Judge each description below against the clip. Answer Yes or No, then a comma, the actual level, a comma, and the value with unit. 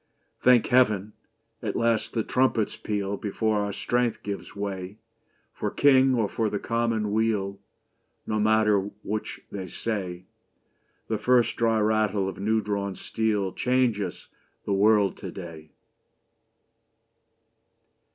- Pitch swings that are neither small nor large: No, narrow, 2.2 semitones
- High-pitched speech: No, low, 105 Hz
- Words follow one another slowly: Yes, slow, 120 wpm